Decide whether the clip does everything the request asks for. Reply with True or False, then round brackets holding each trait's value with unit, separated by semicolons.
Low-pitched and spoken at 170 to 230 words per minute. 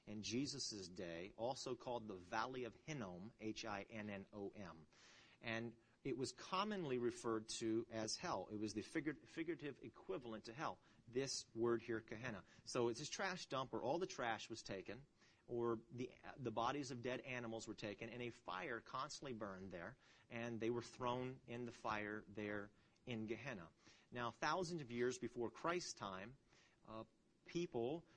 False (115 Hz; 160 wpm)